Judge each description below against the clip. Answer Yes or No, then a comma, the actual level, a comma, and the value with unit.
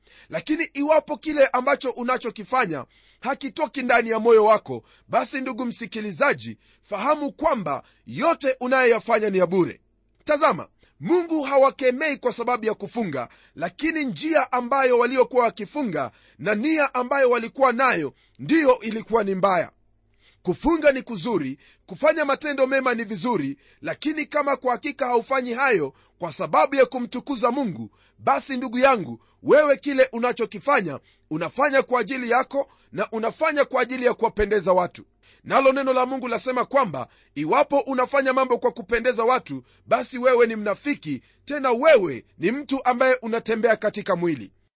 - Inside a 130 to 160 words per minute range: Yes, average, 135 wpm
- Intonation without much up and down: No, average, 4.1 semitones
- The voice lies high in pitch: Yes, very high, 250 Hz